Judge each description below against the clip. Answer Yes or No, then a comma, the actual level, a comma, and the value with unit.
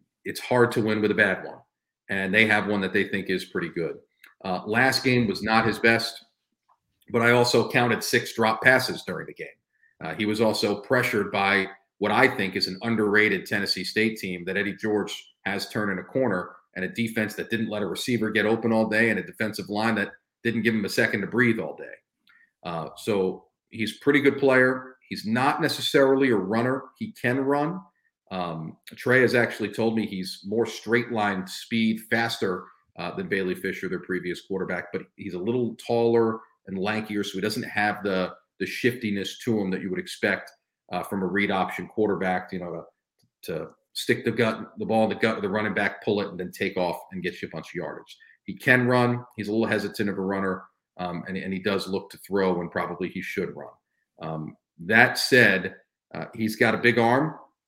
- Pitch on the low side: Yes, low, 110 Hz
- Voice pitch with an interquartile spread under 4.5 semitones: Yes, average, 3.4 semitones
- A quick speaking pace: Yes, fast, 210 wpm